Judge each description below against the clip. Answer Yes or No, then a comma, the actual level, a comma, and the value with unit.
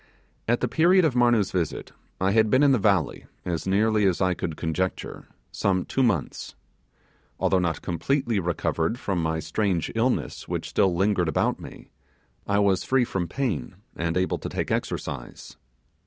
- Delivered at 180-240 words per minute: No, average, 165 wpm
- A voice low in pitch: Yes, very low, 95 Hz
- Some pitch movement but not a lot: Yes, average, 5.0 semitones